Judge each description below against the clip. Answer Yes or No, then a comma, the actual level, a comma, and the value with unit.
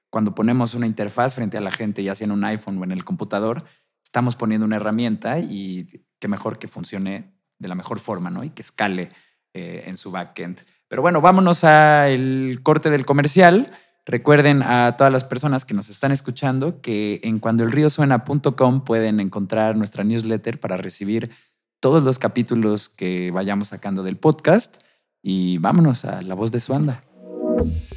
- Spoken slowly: No, average, 170 wpm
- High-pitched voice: No, low, 115 Hz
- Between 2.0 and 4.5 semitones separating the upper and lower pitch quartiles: No, average, 5.0 semitones